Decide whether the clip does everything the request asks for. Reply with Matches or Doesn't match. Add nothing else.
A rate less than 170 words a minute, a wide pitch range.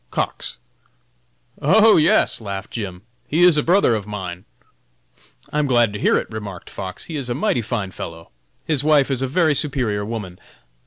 Doesn't match